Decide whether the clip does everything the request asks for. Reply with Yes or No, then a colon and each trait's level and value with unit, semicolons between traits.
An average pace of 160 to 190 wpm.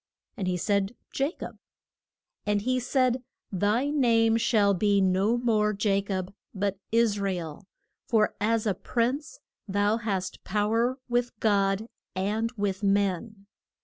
No: average, 145 wpm